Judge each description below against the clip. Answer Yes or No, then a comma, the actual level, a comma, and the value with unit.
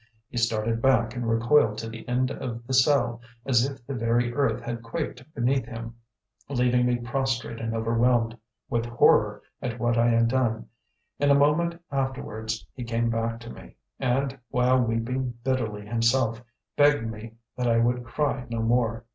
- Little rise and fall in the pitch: Yes, narrow, 2.1 semitones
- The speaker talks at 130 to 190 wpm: Yes, average, 170 wpm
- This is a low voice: Yes, low, 120 Hz